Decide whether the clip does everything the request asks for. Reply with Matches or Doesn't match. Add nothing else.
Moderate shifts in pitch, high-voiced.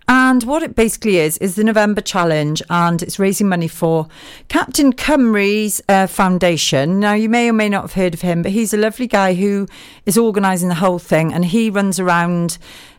Matches